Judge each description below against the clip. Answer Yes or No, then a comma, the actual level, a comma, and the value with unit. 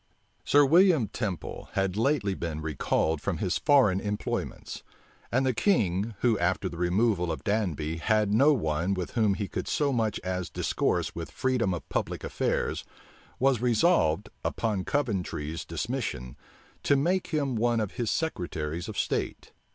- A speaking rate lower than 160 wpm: Yes, average, 150 wpm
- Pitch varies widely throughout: Yes, wide, 6.5 semitones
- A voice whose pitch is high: No, low, 105 Hz